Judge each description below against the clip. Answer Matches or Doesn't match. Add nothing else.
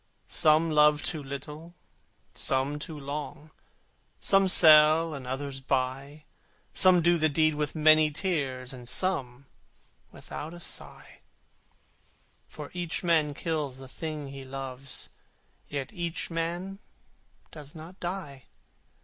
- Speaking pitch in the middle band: Matches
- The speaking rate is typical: Doesn't match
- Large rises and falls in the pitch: Doesn't match